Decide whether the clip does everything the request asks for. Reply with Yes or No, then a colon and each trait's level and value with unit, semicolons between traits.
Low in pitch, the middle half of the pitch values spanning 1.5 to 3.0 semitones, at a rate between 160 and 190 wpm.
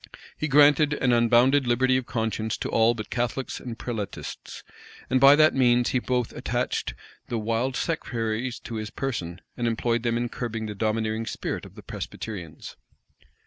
Yes: low, 120 Hz; narrow, 2.6 semitones; average, 165 wpm